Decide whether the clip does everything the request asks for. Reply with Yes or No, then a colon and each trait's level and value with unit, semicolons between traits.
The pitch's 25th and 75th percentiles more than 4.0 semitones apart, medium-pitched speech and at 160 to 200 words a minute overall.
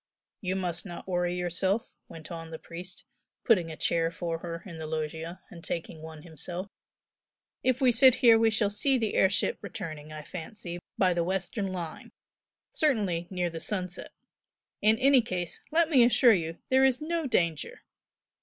Yes: average, 5.1 semitones; medium, 180 Hz; average, 175 wpm